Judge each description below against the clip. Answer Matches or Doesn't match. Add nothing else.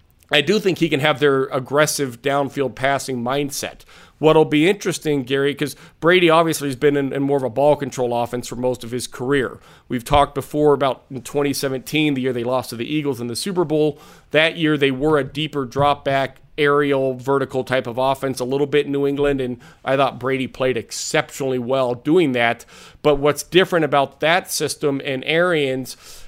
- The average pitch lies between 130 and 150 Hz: Matches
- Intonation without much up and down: Matches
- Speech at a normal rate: Matches